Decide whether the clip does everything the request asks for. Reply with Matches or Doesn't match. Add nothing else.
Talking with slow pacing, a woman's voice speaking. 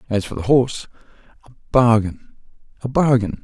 Doesn't match